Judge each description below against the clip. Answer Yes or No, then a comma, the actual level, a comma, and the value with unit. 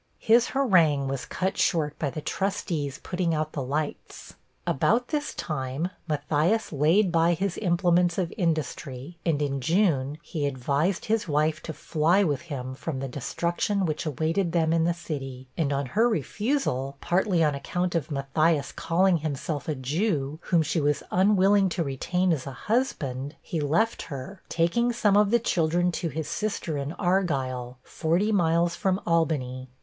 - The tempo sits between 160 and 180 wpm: Yes, average, 165 wpm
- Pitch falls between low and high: Yes, medium, 165 Hz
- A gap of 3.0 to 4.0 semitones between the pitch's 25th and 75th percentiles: No, average, 4.5 semitones